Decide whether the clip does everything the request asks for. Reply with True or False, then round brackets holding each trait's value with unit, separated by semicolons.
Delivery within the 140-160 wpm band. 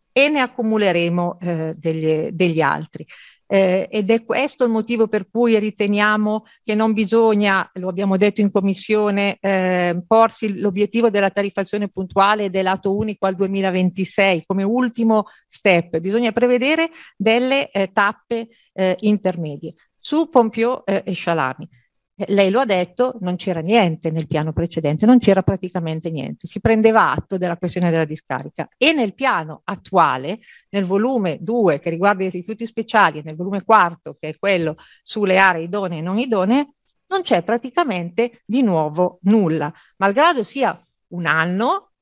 True (150 wpm)